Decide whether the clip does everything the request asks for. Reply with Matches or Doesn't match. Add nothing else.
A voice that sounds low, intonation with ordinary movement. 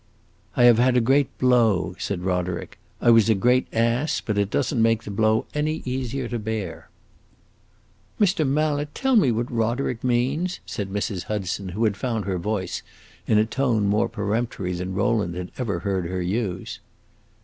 Matches